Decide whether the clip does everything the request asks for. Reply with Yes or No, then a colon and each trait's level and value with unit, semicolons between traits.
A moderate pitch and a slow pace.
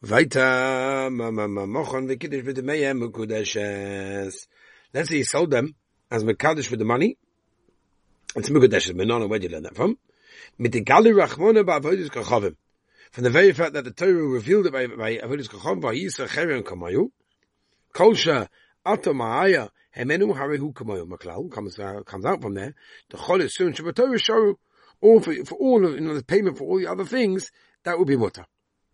Yes: medium, 150 Hz; slow, 115 wpm